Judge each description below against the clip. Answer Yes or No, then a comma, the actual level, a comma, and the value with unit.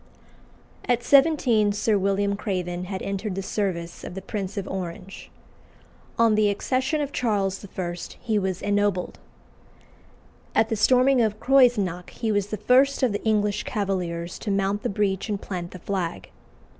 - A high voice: Yes, high, 205 Hz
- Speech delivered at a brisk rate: No, average, 155 wpm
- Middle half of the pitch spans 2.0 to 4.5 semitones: Yes, average, 2.8 semitones